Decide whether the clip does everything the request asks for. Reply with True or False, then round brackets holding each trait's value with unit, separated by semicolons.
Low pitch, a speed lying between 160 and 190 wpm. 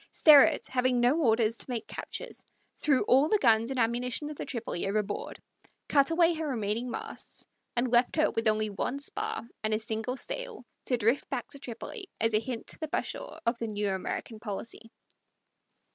False (240 Hz; 185 wpm)